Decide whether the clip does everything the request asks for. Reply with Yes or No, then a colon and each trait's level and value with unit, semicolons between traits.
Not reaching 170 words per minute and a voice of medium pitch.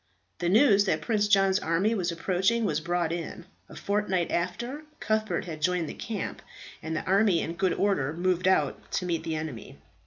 No: average, 185 wpm; medium, 180 Hz